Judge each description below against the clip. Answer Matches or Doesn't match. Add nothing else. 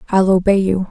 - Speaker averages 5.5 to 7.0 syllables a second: Matches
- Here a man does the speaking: Doesn't match